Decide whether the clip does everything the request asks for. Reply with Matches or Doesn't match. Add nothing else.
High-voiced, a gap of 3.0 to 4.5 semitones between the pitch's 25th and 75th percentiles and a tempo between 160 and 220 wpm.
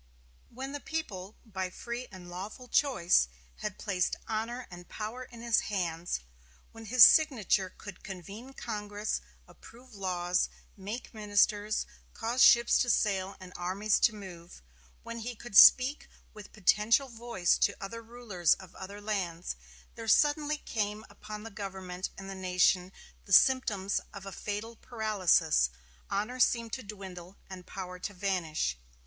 Doesn't match